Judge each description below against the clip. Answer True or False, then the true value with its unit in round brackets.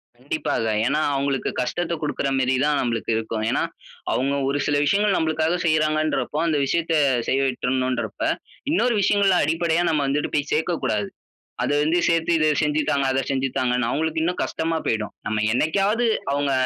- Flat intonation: False (3.8 semitones)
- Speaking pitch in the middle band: True (150 Hz)